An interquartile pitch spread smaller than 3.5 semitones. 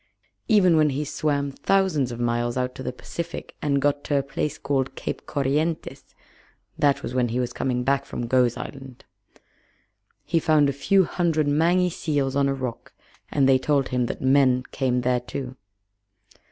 Yes: average, 3.0 semitones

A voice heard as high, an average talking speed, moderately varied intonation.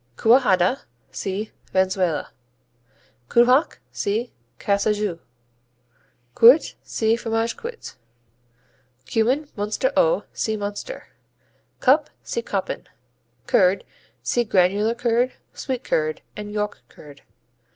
No: high, 220 Hz; slow, 90 wpm; average, 3.6 semitones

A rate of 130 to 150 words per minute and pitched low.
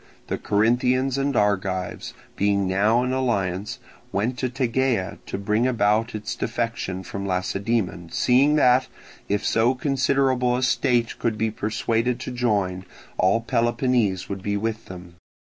Yes: average, 140 wpm; low, 115 Hz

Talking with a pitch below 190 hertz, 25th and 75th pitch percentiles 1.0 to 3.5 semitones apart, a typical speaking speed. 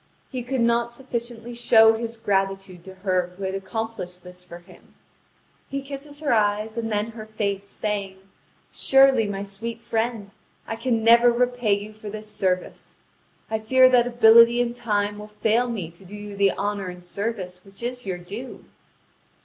No: high, 215 Hz; average, 3.2 semitones; average, 175 wpm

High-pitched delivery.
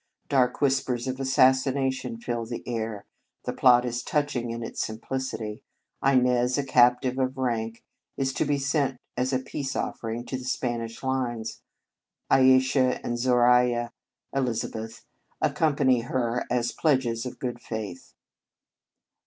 No: low, 125 Hz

